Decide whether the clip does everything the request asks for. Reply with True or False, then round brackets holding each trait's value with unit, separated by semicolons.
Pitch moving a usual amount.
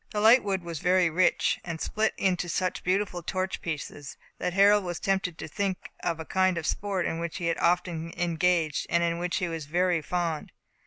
False (2.0 semitones)